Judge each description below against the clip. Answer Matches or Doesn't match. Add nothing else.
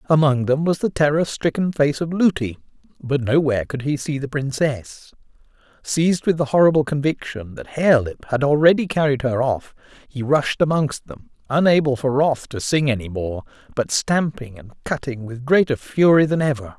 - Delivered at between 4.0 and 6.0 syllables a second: Matches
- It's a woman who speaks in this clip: Doesn't match